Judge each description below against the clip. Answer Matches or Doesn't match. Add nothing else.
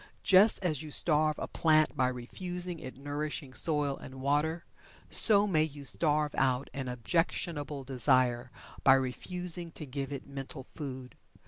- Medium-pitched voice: Matches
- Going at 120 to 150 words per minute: Matches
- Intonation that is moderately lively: Matches